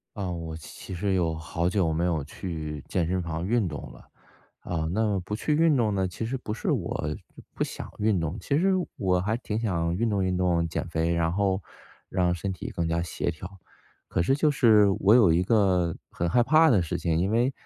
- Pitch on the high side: No, very low, 90 Hz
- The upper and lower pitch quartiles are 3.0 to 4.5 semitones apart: Yes, average, 4.2 semitones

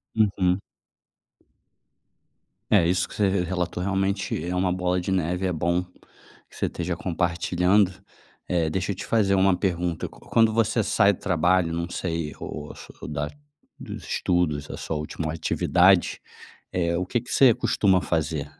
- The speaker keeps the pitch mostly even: Yes, narrow, 2.3 semitones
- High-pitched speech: No, very low, 90 Hz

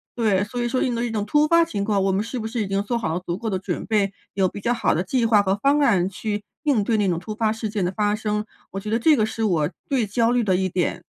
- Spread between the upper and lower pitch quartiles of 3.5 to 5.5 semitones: No, average, 3.1 semitones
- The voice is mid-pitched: No, high, 210 Hz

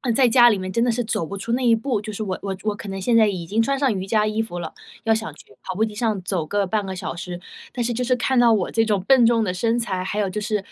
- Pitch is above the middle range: Yes, high, 215 Hz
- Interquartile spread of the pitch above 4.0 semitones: No, average, 3.3 semitones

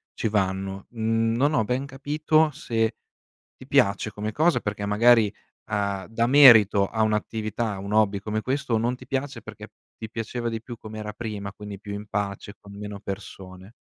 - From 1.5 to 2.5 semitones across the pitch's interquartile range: No, average, 2.9 semitones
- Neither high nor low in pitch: No, low, 110 Hz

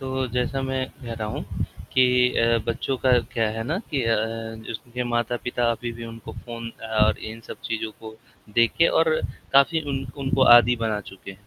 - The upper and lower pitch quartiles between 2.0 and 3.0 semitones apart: Yes, narrow, 2.6 semitones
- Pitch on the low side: Yes, low, 120 Hz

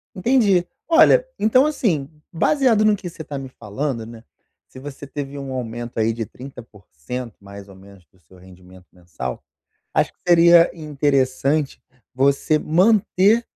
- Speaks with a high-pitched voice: No, low, 135 Hz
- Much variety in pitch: Yes, wide, 7.7 semitones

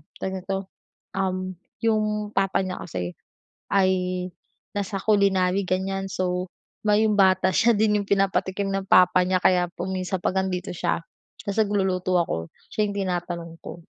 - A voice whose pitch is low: No, high, 190 Hz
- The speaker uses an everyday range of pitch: No, narrow, 1.5 semitones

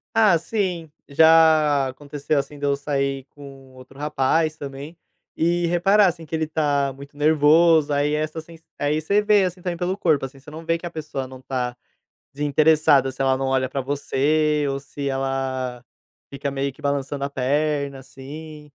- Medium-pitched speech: Yes, medium, 145 Hz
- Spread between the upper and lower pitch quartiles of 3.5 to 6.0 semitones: No, average, 2.7 semitones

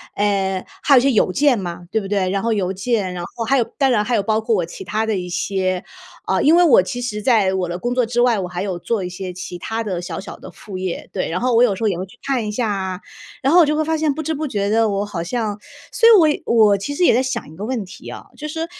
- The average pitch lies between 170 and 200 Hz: No, high, 215 Hz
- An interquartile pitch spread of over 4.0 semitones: Yes, average, 4.9 semitones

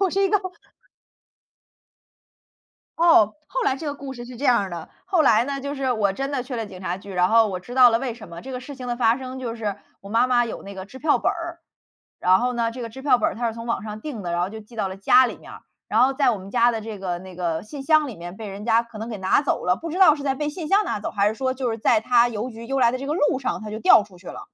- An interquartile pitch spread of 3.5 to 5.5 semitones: Yes, average, 4.4 semitones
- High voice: Yes, high, 235 Hz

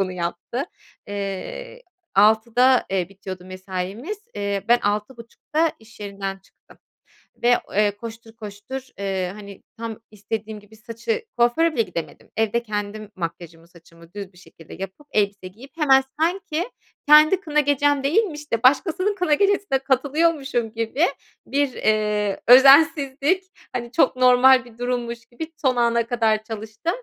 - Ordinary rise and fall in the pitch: No, wide, 5.7 semitones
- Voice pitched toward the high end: Yes, high, 230 Hz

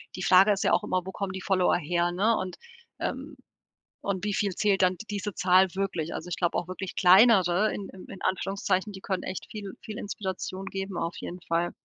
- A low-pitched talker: No, high, 190 Hz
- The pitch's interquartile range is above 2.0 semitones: No, narrow, 1.7 semitones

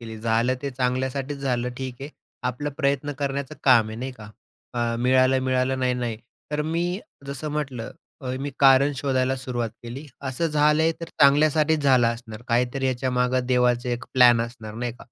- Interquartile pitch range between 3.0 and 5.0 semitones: No, narrow, 2.4 semitones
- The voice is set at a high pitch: No, low, 130 Hz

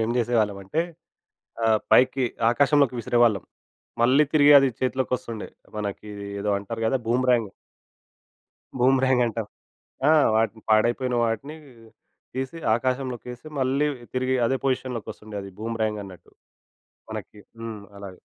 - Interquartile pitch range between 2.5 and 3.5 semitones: Yes, average, 3.1 semitones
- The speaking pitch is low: Yes, low, 120 Hz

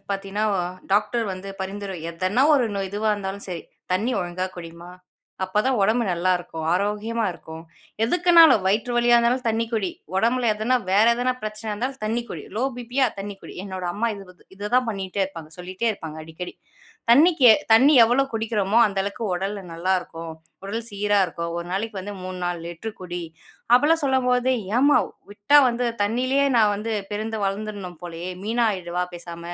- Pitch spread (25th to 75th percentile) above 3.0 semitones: Yes, average, 4.2 semitones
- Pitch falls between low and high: No, high, 205 Hz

